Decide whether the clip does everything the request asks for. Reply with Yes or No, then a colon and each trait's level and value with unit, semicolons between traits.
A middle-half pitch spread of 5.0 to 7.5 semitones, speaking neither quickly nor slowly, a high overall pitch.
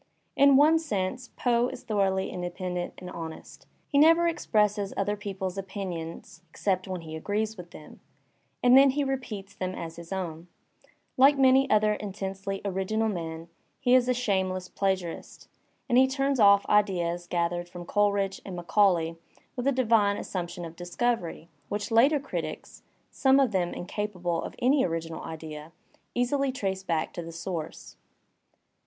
Yes: wide, 5.5 semitones; average, 155 wpm; high, 195 Hz